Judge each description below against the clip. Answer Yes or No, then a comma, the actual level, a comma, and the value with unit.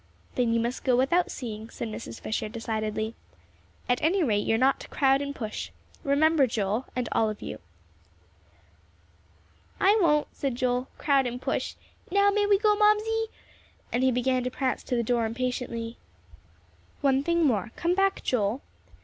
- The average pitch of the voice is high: Yes, very high, 255 Hz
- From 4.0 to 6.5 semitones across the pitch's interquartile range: Yes, average, 5.1 semitones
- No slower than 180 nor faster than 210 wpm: No, average, 165 wpm